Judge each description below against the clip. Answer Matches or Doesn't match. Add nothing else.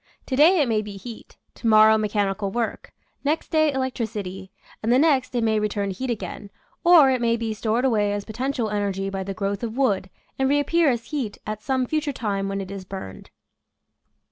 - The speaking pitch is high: Matches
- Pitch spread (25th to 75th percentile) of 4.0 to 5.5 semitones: Matches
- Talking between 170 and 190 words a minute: Doesn't match